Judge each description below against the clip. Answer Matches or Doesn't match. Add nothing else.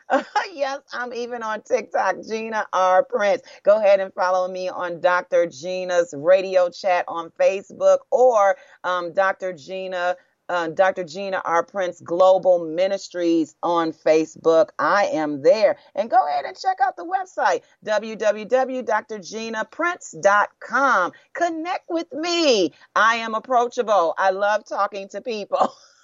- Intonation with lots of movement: Matches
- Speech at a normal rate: Doesn't match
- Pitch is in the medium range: Doesn't match